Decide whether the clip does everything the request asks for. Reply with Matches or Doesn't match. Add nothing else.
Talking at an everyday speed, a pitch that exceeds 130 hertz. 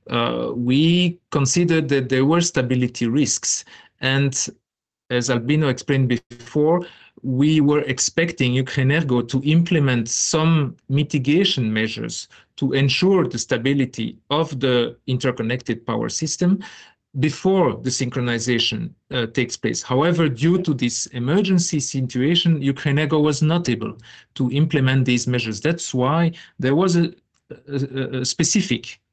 Matches